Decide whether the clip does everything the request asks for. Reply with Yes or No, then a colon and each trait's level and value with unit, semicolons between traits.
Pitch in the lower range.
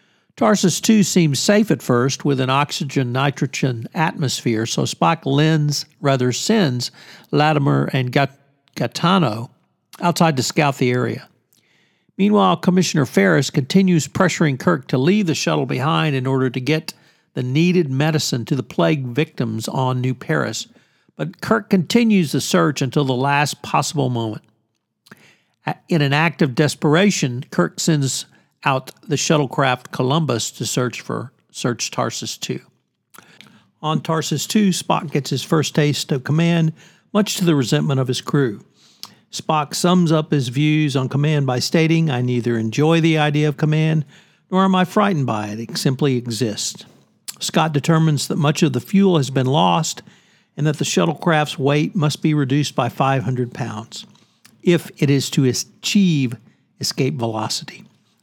No: medium, 150 Hz